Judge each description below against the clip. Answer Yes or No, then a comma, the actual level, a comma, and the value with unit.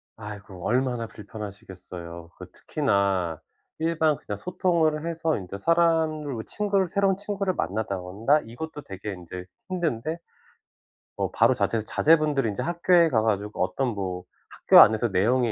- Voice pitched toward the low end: Yes, low, 120 Hz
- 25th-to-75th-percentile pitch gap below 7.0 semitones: No, wide, 8.6 semitones